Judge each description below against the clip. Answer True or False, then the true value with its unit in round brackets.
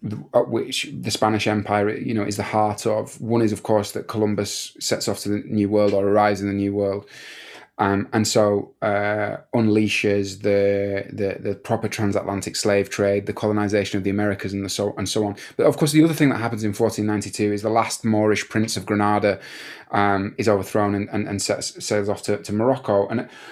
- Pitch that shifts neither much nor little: False (1.2 semitones)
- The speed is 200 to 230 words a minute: True (205 wpm)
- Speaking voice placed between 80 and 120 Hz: True (105 Hz)